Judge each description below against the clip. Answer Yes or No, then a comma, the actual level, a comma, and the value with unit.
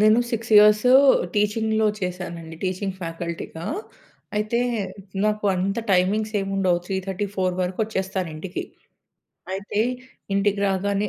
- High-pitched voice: Yes, high, 195 Hz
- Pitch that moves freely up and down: No, narrow, 2.4 semitones